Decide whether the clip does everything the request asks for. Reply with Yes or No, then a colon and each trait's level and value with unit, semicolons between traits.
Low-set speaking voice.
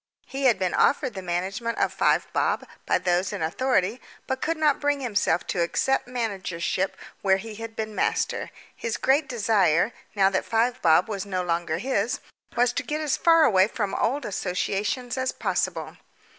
No: high, 220 Hz